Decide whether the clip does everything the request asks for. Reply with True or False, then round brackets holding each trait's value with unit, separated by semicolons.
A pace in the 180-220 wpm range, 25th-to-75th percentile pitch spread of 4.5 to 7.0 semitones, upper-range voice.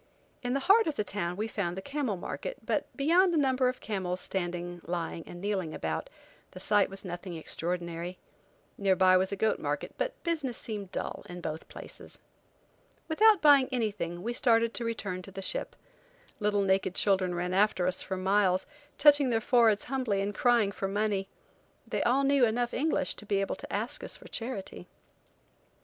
True (185 wpm; 5.3 semitones; 205 Hz)